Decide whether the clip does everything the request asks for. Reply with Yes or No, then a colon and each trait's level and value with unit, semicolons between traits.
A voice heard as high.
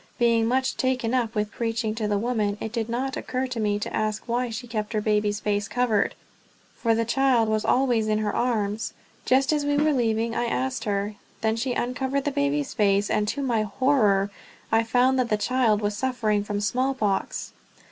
Yes: high, 230 Hz